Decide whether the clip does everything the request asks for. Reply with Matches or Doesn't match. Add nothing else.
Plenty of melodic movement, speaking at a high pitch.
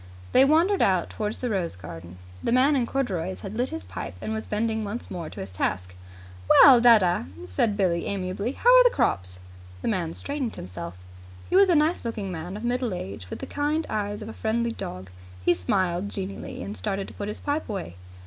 Matches